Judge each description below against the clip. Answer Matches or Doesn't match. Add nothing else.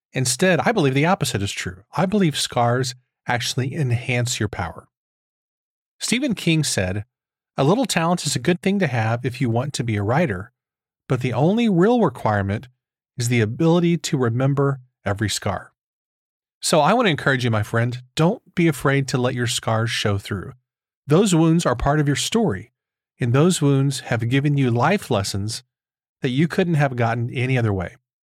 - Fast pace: Doesn't match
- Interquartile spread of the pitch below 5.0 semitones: Doesn't match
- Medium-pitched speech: Doesn't match